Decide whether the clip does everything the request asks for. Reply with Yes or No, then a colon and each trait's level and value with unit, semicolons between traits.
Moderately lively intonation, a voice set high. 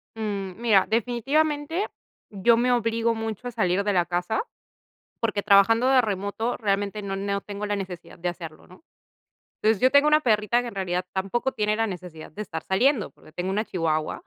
Yes: average, 3.6 semitones; high, 210 Hz